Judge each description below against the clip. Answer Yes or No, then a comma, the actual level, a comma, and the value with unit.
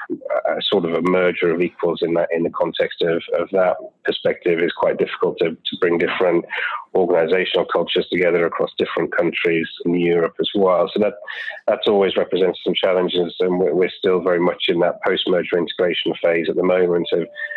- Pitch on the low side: No, very high, 325 Hz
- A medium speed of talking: Yes, average, 185 wpm